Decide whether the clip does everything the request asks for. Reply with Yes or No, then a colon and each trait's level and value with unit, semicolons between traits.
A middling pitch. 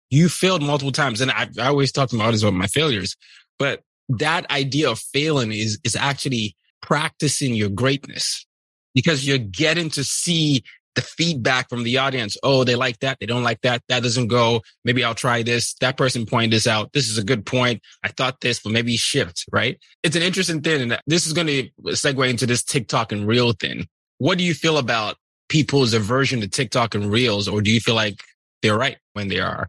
No: low, 125 Hz